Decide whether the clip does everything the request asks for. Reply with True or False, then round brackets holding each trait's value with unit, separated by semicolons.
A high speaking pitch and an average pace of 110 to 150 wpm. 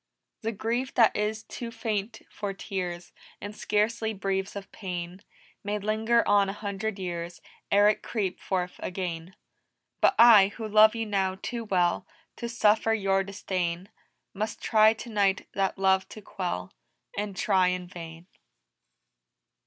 True (200 Hz; 145 wpm)